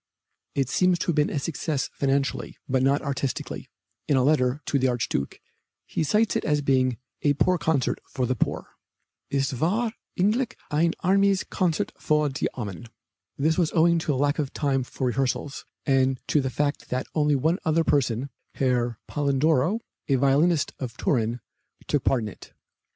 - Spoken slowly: No, average, 170 wpm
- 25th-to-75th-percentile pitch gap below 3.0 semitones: No, average, 3.5 semitones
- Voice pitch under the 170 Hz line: Yes, medium, 140 Hz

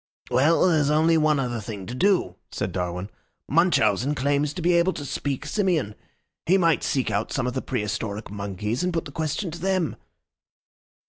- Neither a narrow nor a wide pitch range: No, wide, 6.9 semitones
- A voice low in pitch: No, medium, 145 Hz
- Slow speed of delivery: No, average, 185 wpm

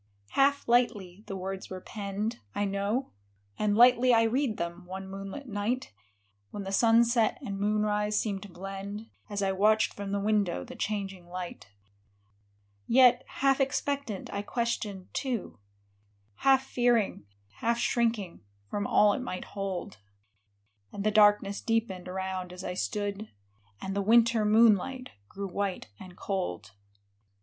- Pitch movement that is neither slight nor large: Yes, average, 3.2 semitones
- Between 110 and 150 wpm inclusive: Yes, average, 140 wpm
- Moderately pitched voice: No, high, 205 Hz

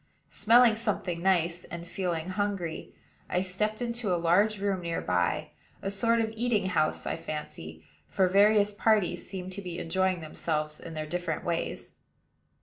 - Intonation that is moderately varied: Yes, average, 3.6 semitones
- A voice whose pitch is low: No, medium, 185 Hz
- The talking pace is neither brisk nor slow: Yes, average, 155 wpm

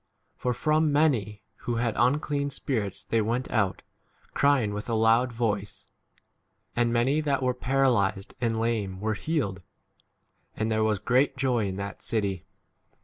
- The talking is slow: No, average, 160 wpm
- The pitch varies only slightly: No, average, 3.9 semitones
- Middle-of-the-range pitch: No, low, 115 Hz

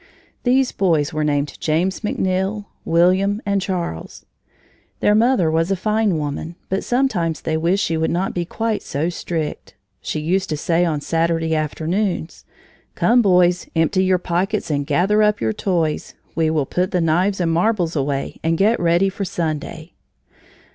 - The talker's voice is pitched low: No, medium, 175 Hz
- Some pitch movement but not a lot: Yes, average, 3.4 semitones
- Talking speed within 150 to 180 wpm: Yes, average, 160 wpm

